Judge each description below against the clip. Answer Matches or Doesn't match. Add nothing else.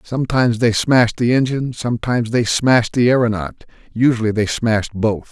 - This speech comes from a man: Matches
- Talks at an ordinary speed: Matches